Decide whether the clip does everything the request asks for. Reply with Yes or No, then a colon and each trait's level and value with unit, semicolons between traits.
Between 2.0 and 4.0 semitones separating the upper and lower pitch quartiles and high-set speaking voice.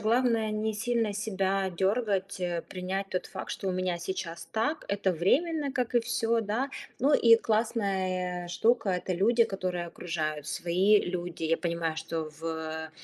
No: average, 4.4 semitones; high, 195 Hz